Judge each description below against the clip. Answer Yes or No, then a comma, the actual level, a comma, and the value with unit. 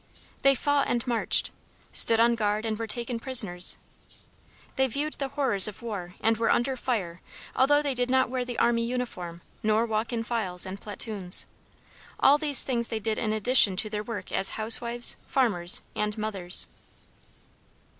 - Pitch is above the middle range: Yes, high, 230 Hz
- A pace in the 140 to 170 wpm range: Yes, average, 165 wpm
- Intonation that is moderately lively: Yes, average, 3.1 semitones